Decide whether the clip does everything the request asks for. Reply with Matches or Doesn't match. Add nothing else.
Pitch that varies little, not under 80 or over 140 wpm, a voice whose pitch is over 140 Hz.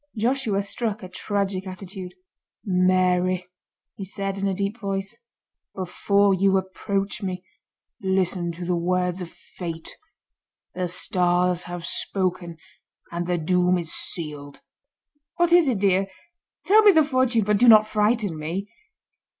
Matches